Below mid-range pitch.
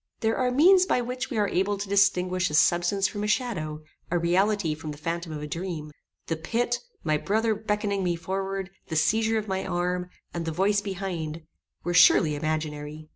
No: medium, 185 Hz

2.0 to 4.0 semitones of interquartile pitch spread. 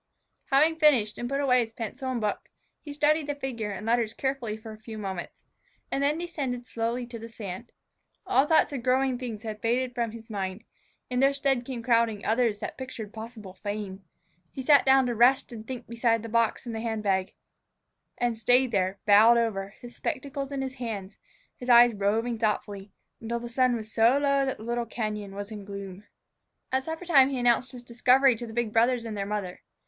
Yes: average, 3.3 semitones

